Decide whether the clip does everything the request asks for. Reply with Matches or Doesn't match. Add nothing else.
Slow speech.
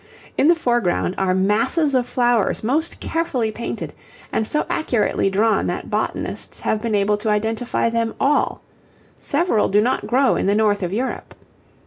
Doesn't match